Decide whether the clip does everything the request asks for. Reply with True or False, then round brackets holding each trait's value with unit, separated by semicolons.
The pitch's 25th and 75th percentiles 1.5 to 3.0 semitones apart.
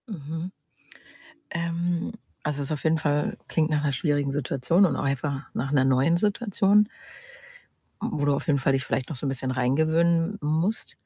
False (3.6 semitones)